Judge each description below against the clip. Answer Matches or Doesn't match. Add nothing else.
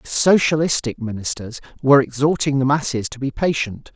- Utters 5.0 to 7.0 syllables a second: Matches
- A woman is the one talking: Doesn't match